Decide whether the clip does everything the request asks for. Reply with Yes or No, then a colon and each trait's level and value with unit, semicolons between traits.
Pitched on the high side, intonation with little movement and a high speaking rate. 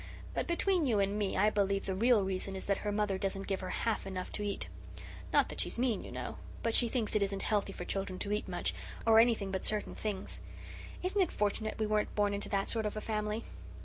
Yes: high, 210 Hz; narrow, 2.1 semitones; fast, 240 wpm